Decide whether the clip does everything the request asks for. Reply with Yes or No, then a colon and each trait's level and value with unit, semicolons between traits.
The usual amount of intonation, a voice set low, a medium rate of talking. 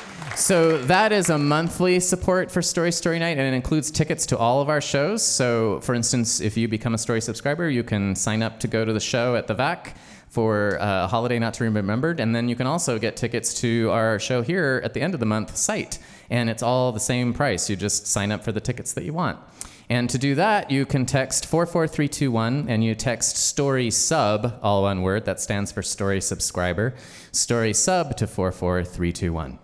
No: average, 4.9 semitones; low, 120 Hz; fast, 215 wpm